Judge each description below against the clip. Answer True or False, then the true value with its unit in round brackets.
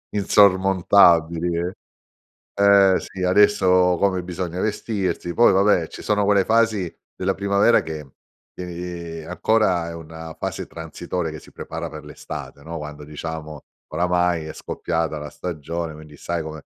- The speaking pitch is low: True (90 Hz)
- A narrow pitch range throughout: False (3.0 semitones)